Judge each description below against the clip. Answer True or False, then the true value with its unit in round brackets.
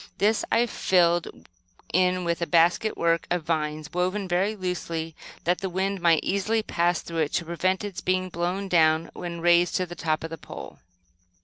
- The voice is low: False (175 Hz)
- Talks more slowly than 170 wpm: False (185 wpm)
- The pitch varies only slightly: True (2.0 semitones)